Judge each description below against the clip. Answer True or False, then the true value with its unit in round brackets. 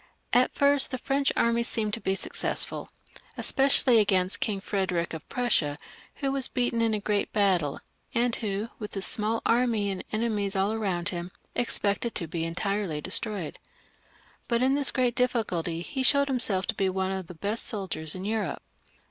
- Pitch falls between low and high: False (210 Hz)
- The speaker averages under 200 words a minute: True (175 wpm)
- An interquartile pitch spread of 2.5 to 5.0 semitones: True (4.1 semitones)